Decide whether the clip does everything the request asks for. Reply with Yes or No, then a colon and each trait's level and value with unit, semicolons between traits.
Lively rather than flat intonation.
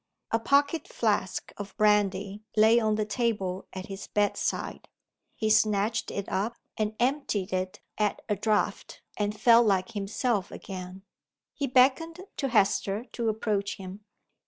No: average, 2.9 semitones